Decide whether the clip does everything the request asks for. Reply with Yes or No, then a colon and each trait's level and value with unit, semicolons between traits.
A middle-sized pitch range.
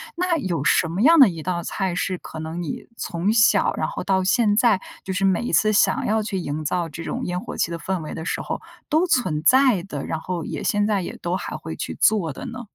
Yes: average, 4.7 semitones